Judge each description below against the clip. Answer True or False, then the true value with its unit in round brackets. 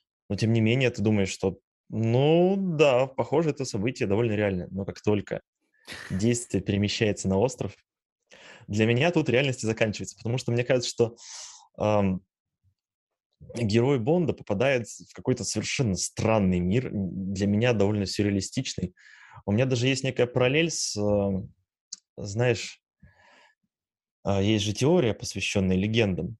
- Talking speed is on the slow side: False (135 wpm)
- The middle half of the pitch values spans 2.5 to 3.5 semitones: False (3.9 semitones)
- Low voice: True (110 Hz)